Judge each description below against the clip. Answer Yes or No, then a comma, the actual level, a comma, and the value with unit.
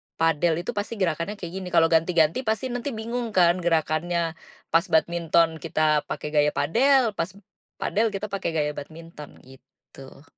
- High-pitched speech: No, medium, 170 Hz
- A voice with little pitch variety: No, average, 4.4 semitones